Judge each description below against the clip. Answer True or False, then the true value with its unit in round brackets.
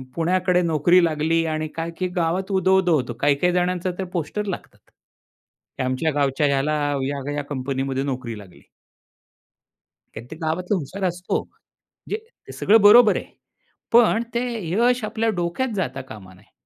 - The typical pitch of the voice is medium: True (165 Hz)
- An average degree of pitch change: True (5.0 semitones)